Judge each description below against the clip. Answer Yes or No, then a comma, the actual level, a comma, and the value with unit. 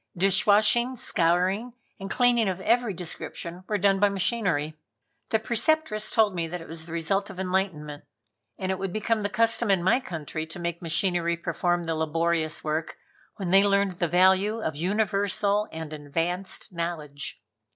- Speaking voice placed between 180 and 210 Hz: Yes, medium, 185 Hz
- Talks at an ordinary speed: Yes, average, 160 wpm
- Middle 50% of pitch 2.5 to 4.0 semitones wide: Yes, average, 3.5 semitones